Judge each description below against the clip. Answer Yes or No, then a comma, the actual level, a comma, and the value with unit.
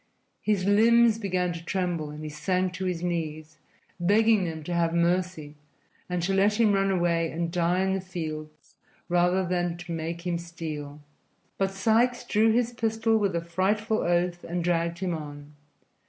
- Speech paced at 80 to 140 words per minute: No, average, 170 wpm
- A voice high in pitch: No, medium, 175 Hz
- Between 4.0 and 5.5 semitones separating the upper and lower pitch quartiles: No, average, 2.7 semitones